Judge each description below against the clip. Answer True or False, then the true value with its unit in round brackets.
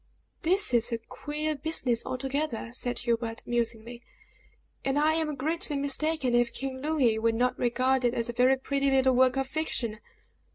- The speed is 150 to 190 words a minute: True (165 wpm)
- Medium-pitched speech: False (260 Hz)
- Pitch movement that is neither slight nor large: True (3.5 semitones)